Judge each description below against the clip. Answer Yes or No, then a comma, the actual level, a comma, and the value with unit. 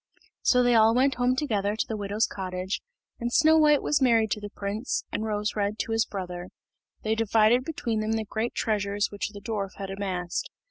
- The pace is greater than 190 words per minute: Yes, average, 200 wpm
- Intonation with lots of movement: No, average, 2.8 semitones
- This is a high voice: Yes, high, 215 Hz